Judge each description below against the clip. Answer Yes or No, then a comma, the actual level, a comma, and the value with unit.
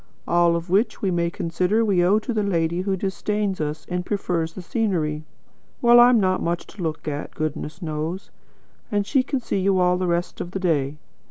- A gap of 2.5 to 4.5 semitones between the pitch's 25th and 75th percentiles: Yes, average, 3.3 semitones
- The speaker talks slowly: No, average, 200 wpm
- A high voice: No, medium, 180 Hz